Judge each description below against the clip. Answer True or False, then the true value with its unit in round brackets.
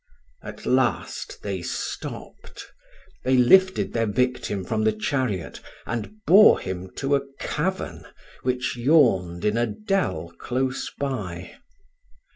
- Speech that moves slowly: True (115 wpm)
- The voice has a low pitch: True (125 Hz)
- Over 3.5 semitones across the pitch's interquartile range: True (5.2 semitones)